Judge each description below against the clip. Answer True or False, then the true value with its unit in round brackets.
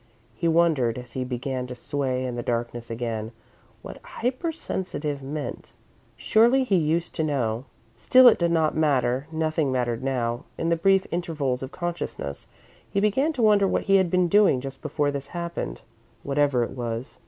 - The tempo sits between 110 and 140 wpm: False (170 wpm)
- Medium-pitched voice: True (145 Hz)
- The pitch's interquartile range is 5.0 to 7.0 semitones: True (5.5 semitones)